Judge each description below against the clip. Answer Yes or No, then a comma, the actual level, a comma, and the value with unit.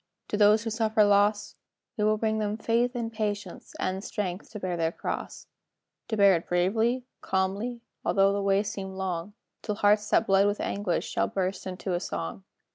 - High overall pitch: Yes, high, 205 Hz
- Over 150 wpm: Yes, average, 185 wpm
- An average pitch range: No, narrow, 2.3 semitones